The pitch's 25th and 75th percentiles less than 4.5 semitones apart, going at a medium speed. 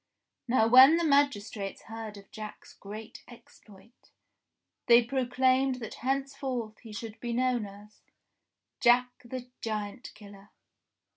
No: average, 3.3 semitones; slow, 125 wpm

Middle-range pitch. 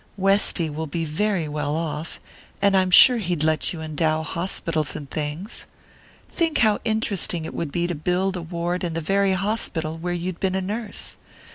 Yes: medium, 175 Hz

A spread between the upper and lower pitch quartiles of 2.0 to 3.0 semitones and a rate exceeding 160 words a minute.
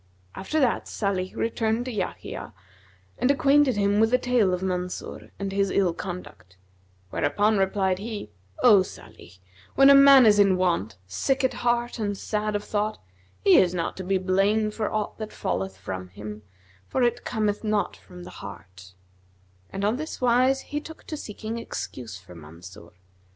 No: average, 4.7 semitones; average, 170 wpm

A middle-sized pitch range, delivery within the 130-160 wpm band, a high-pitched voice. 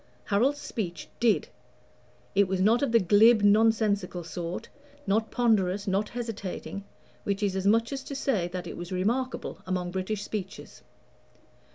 Yes: average, 3.4 semitones; average, 150 wpm; high, 205 Hz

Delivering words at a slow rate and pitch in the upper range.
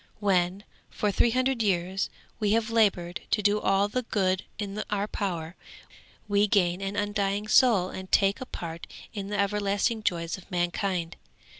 No: average, 160 wpm; high, 200 Hz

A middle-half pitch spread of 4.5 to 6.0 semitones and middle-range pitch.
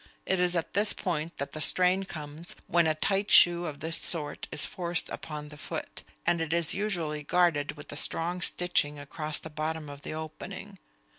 No: average, 2.7 semitones; medium, 160 Hz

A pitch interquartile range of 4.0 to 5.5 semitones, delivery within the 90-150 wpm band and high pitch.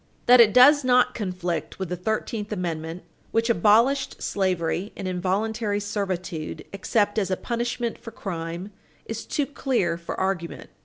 Yes: average, 4.3 semitones; average, 145 wpm; high, 205 Hz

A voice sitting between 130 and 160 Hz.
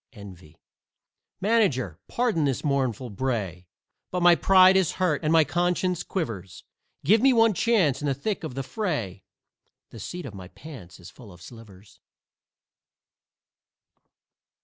Yes: medium, 140 Hz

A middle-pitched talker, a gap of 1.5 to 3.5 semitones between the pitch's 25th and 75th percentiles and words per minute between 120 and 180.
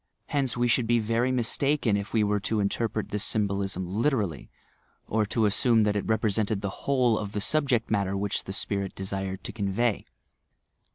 No: low, 105 Hz; average, 3.0 semitones; average, 175 wpm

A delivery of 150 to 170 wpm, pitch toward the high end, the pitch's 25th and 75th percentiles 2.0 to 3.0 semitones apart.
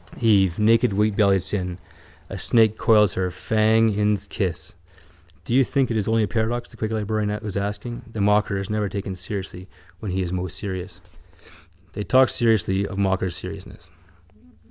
No: average, 165 wpm; low, 105 Hz; narrow, 2.6 semitones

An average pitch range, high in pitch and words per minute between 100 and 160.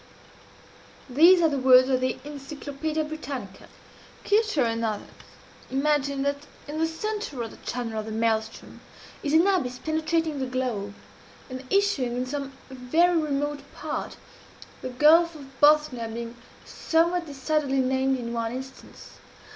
Yes: average, 3.8 semitones; very high, 275 Hz; average, 140 wpm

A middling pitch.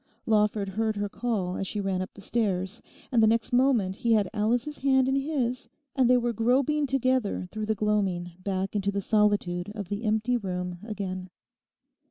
No: high, 215 Hz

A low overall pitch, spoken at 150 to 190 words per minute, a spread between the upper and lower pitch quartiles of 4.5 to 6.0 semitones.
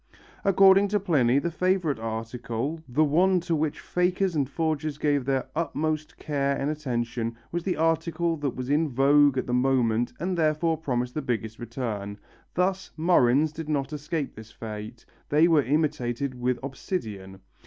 No: medium, 145 Hz; average, 160 wpm; average, 4.9 semitones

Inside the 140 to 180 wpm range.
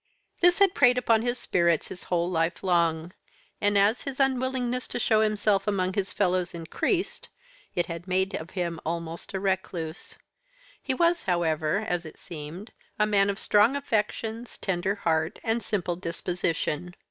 Yes: average, 160 wpm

